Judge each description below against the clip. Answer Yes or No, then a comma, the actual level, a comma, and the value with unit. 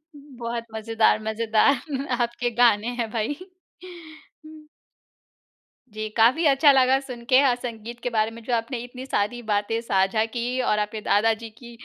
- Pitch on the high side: Yes, high, 235 Hz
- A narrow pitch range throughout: No, average, 3.3 semitones